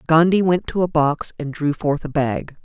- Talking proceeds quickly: Yes, fast, 225 wpm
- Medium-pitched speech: Yes, medium, 155 Hz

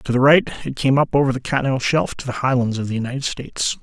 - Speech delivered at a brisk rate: Yes, fast, 265 wpm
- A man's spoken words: Yes, male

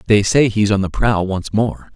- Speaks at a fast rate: Yes, fast, 245 wpm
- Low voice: Yes, low, 105 Hz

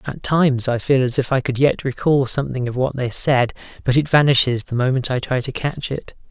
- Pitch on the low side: Yes, low, 130 Hz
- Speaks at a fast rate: Yes, fast, 240 wpm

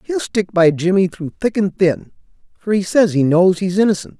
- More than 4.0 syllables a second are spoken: Yes, 5.0 syllables/s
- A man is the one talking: Yes, male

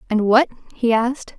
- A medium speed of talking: Yes, average, 175 wpm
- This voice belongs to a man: No, female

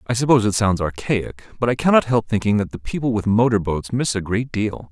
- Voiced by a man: Yes, male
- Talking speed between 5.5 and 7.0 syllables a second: Yes, 5.8 syllables/s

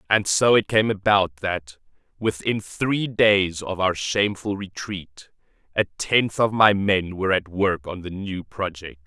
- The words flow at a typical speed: Yes, average, 165 wpm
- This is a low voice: Yes, very low, 95 Hz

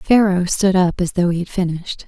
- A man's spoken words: No, female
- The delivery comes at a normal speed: No, fast, 230 wpm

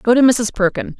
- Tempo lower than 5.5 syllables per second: No, 5.6 syllables/s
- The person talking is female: Yes, female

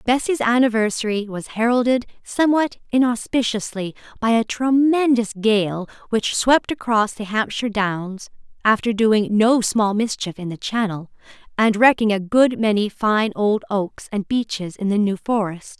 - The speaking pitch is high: Yes, high, 220 Hz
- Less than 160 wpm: Yes, average, 145 wpm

